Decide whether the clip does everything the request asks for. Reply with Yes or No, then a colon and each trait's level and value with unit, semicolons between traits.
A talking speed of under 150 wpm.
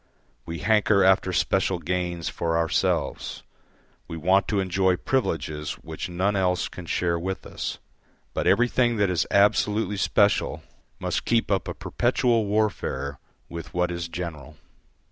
Yes: average, 140 wpm